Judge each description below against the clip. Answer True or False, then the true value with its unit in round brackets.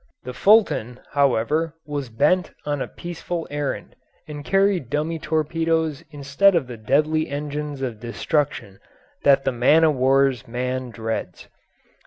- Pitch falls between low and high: True (145 Hz)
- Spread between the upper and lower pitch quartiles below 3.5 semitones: False (3.8 semitones)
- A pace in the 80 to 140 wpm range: True (135 wpm)